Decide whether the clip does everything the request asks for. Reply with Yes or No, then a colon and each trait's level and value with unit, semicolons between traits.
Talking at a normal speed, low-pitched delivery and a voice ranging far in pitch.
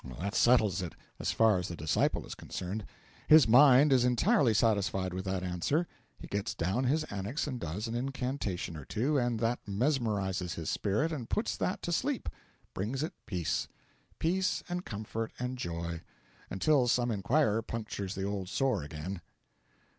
Yes: average, 165 wpm; low, 110 Hz; wide, 5.8 semitones